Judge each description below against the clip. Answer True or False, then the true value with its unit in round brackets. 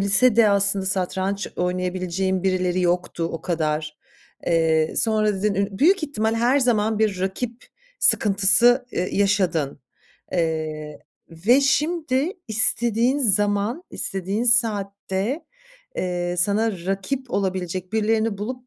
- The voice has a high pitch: True (200 Hz)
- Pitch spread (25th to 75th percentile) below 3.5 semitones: False (3.9 semitones)